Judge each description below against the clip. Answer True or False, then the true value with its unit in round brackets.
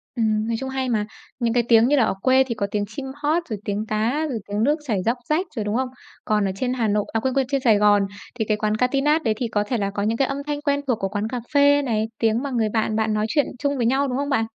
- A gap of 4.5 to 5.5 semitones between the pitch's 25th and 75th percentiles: False (4.0 semitones)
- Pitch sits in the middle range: False (235 Hz)